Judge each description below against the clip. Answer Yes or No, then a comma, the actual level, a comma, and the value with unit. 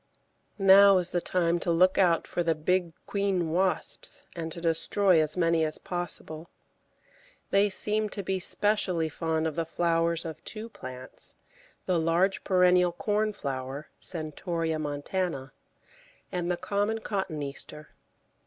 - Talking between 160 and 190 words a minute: No, slow, 135 wpm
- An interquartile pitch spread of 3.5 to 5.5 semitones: No, average, 3.0 semitones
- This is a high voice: No, medium, 175 Hz